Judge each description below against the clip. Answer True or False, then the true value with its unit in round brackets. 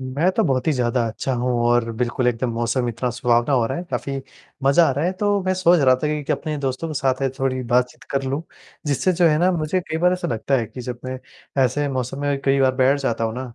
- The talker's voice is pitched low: True (130 Hz)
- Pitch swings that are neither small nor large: True (3.5 semitones)